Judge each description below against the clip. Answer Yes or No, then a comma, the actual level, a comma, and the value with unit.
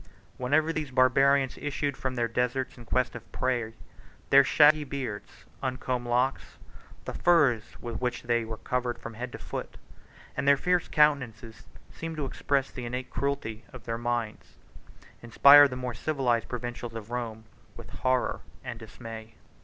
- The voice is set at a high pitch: No, low, 125 Hz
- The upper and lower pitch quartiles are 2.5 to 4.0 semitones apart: Yes, average, 2.9 semitones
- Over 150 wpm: Yes, average, 160 wpm